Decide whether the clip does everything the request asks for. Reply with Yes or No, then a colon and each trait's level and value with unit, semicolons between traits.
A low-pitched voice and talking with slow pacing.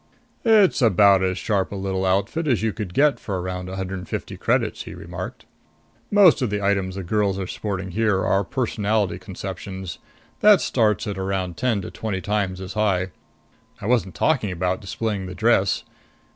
No: low, 100 Hz; average, 180 wpm